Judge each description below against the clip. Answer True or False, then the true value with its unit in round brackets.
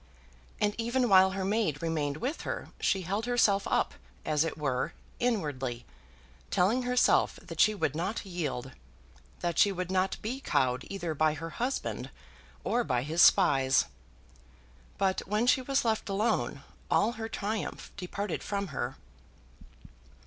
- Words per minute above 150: False (145 wpm)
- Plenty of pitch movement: True (6.1 semitones)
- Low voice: False (190 Hz)